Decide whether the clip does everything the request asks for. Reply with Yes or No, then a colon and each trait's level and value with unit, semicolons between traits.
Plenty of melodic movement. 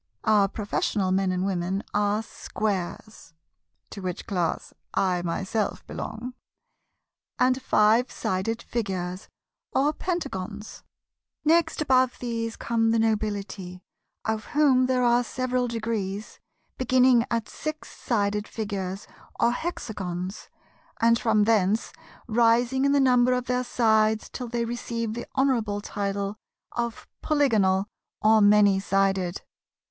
No: average, 3.6 semitones